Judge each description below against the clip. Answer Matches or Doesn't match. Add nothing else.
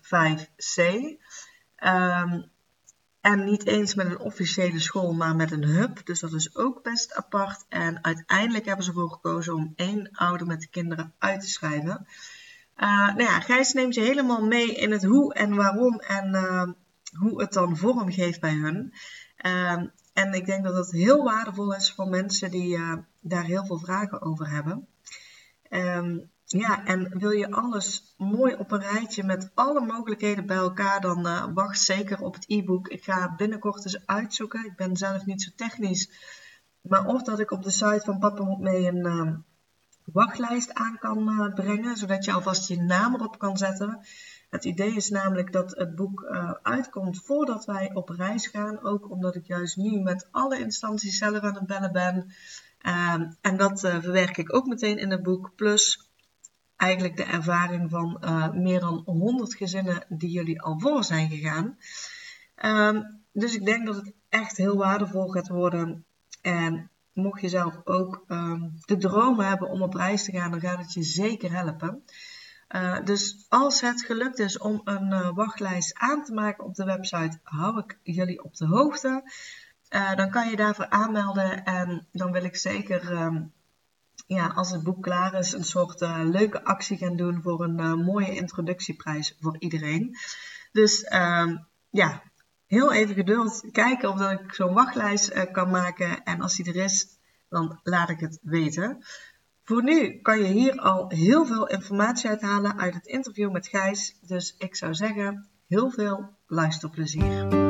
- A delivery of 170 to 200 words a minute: Matches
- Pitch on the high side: Matches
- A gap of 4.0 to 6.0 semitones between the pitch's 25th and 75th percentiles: Doesn't match